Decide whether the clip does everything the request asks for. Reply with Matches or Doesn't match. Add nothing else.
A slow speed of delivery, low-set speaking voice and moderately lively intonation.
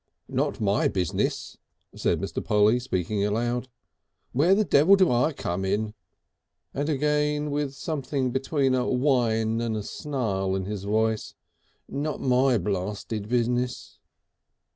Matches